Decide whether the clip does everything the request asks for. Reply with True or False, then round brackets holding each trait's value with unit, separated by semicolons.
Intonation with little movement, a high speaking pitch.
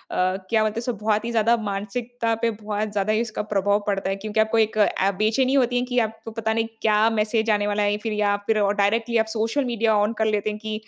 True (1.5 semitones; 215 Hz)